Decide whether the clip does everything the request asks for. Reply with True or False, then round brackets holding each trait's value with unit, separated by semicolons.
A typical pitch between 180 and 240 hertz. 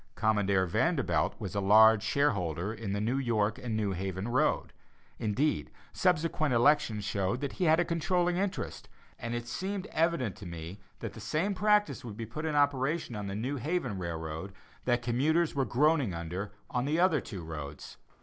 False (120 Hz)